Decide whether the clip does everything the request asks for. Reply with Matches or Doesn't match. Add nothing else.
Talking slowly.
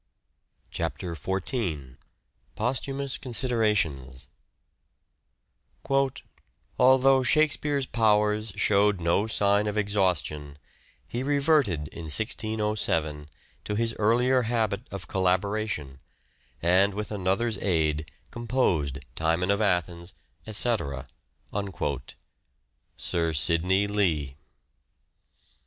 Matches